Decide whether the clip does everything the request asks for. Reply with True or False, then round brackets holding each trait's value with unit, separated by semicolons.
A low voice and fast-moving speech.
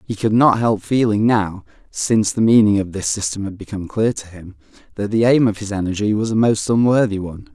True (105 Hz; 225 wpm)